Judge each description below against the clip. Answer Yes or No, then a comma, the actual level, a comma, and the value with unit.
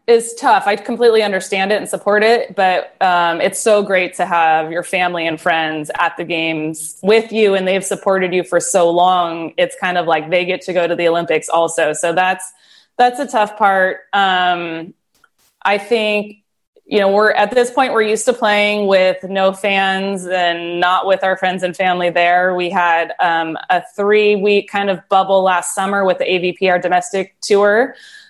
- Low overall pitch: No, high, 190 Hz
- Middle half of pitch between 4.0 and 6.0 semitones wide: No, average, 2.8 semitones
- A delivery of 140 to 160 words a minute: No, average, 195 wpm